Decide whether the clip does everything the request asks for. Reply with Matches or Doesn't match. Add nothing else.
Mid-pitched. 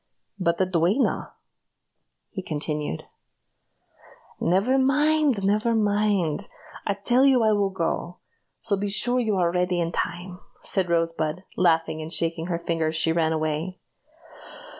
Matches